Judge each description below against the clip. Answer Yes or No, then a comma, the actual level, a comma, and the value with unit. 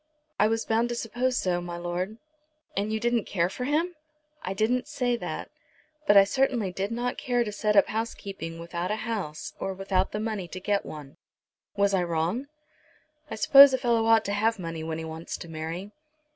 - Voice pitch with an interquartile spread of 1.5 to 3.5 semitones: No, average, 4.7 semitones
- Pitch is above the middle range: Yes, high, 205 Hz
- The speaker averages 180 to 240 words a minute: Yes, average, 200 wpm